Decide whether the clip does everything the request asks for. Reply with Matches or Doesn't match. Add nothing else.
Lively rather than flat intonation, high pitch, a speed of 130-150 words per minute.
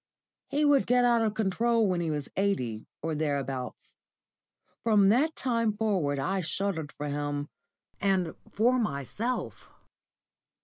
Matches